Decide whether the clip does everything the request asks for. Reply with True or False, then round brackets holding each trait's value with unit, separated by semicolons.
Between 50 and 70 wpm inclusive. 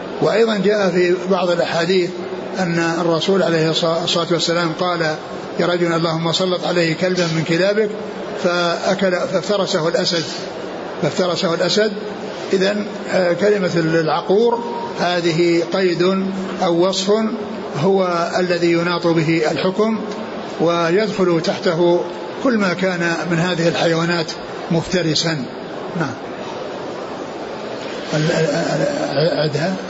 False (90 wpm)